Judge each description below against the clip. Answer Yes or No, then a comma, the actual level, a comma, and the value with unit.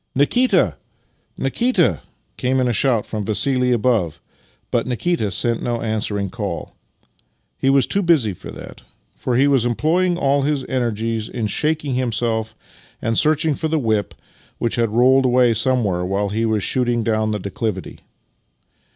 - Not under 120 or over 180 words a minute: Yes, average, 160 wpm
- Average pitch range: Yes, average, 3.9 semitones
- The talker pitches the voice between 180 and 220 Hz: No, low, 120 Hz